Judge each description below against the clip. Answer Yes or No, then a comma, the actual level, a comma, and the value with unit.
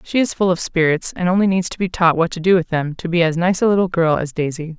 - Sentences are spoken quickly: Yes, fast, 315 wpm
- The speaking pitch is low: No, medium, 175 Hz